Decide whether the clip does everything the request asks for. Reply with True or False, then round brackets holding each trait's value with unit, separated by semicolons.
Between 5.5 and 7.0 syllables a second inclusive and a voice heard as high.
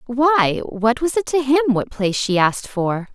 False (4.6 syllables/s; 250 Hz)